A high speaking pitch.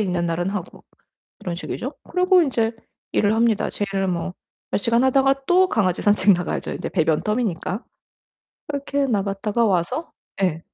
Yes: high, 210 Hz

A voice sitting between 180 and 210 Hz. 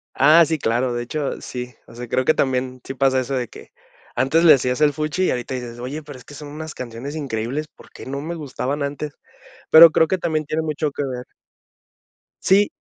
No: medium, 140 Hz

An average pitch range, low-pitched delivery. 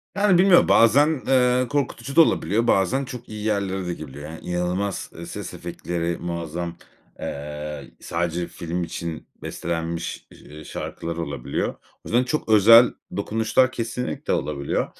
No: wide, 6.8 semitones; very low, 95 Hz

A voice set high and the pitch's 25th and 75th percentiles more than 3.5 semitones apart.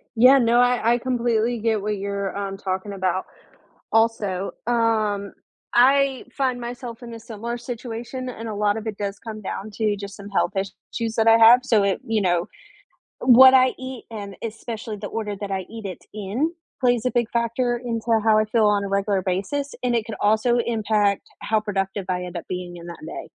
No: high, 220 Hz; average, 3.0 semitones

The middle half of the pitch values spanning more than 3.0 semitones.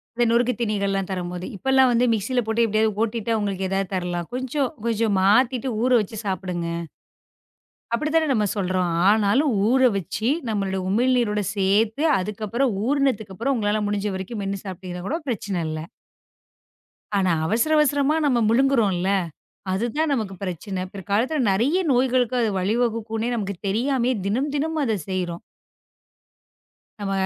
Yes: average, 4.4 semitones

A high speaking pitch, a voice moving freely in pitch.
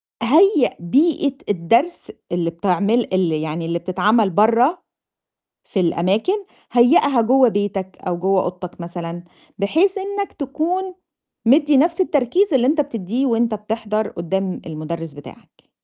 Yes: high, 220 Hz; wide, 8.1 semitones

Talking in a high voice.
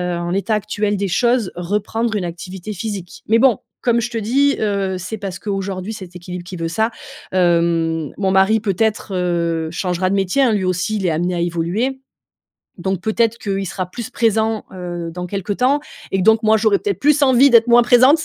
Yes: high, 195 Hz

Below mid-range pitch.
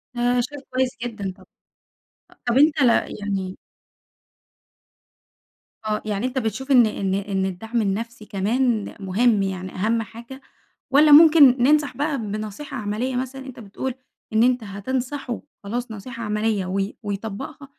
No: high, 230 Hz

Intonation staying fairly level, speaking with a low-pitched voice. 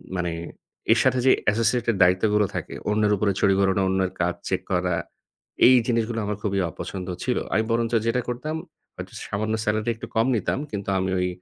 No: average, 3.4 semitones; low, 105 Hz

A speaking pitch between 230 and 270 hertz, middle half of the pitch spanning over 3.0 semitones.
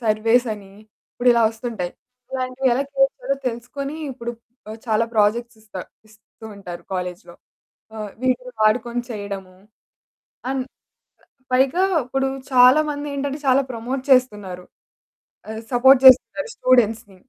Yes: high, 240 Hz; average, 3.5 semitones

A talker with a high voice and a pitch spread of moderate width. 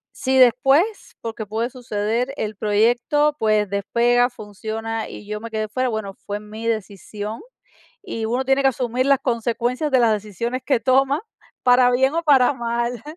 Yes: high, 235 Hz; average, 3.1 semitones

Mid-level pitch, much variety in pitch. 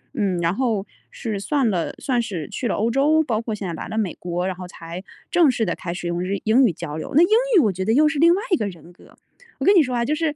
No: high, 220 Hz; wide, 7.2 semitones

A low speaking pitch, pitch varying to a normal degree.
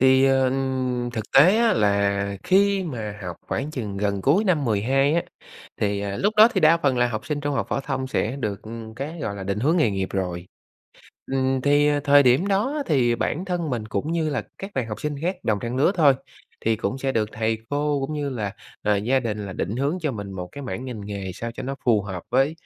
No: low, 130 Hz; wide, 5.9 semitones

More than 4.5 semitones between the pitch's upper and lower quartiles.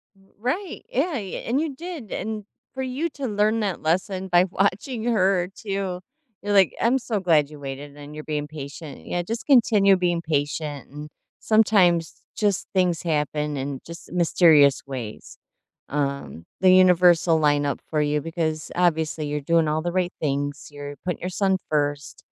Yes: average, 5.2 semitones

